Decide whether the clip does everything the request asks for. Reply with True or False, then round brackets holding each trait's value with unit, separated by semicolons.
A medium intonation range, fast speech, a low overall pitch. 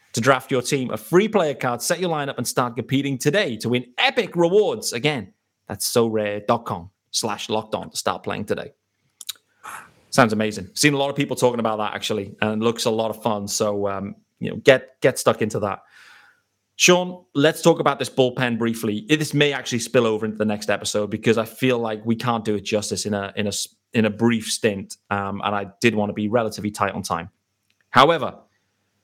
True (4.4 semitones; 215 wpm; 115 Hz)